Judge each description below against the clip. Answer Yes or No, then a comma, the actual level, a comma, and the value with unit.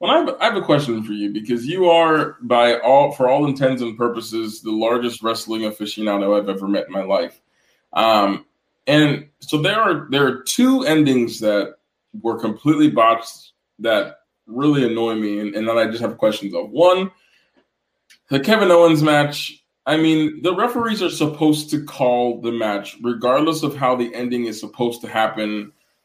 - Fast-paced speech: No, average, 175 wpm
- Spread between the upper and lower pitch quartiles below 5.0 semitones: No, average, 5.3 semitones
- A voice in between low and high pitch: No, low, 125 Hz